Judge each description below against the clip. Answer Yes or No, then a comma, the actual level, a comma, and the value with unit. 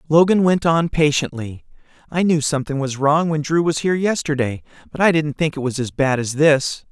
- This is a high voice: No, medium, 150 Hz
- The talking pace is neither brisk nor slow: No, fast, 210 wpm